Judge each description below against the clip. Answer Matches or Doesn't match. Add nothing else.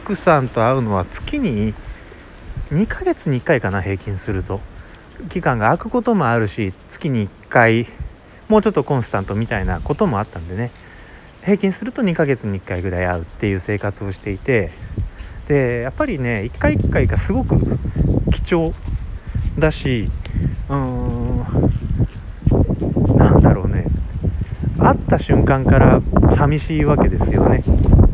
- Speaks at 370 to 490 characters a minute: Doesn't match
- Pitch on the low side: Matches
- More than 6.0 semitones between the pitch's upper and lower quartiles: Matches